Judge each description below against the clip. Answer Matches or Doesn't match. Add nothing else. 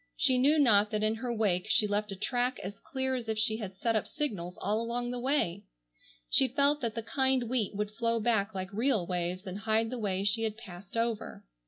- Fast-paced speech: Matches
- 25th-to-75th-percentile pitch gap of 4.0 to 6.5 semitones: Doesn't match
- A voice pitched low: Doesn't match